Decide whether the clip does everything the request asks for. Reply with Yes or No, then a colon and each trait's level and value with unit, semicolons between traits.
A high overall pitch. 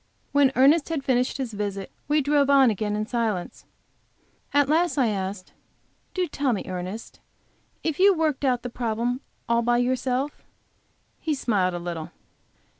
Yes: very high, 250 Hz